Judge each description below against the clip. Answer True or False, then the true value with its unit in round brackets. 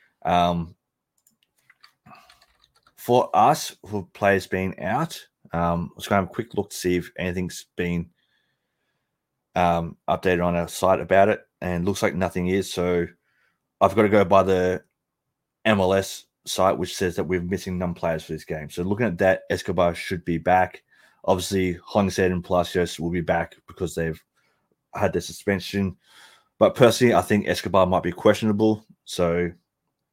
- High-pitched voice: False (90 Hz)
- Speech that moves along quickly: False (165 wpm)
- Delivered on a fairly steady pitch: True (1.9 semitones)